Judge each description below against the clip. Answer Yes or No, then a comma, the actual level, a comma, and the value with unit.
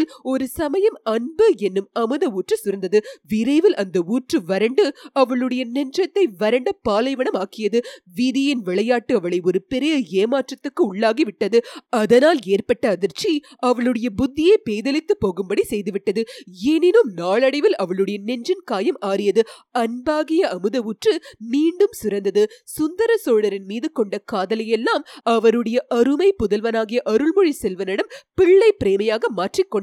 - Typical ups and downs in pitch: No, wide, 6.6 semitones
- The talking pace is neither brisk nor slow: Yes, average, 110 wpm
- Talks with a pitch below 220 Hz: No, high, 245 Hz